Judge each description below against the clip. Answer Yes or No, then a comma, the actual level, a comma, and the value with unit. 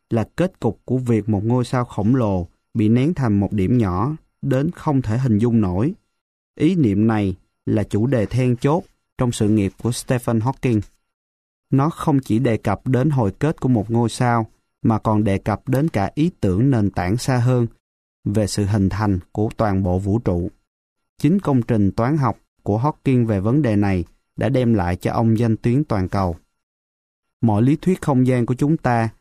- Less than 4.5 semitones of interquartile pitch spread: Yes, average, 4.1 semitones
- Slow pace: No, average, 200 wpm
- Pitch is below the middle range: Yes, low, 115 Hz